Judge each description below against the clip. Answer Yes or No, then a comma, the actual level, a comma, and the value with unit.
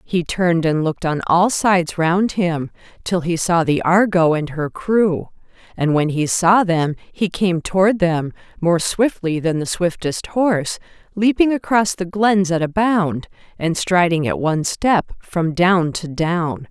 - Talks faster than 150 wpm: Yes, average, 170 wpm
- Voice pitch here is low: No, medium, 175 Hz